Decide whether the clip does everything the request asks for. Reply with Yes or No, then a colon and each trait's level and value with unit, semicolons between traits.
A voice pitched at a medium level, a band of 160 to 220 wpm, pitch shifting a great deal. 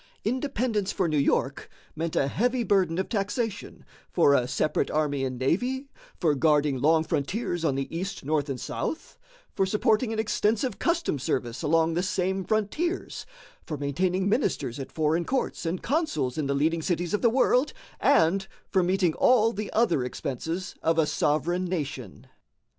Yes: medium, 175 Hz; average, 165 wpm; wide, 6.4 semitones